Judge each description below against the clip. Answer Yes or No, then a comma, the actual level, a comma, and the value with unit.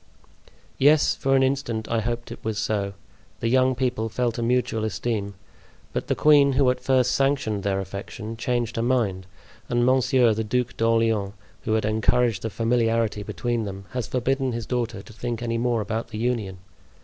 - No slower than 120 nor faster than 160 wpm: No, average, 180 wpm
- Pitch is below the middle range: Yes, low, 115 Hz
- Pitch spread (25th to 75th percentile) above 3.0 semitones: No, narrow, 2.4 semitones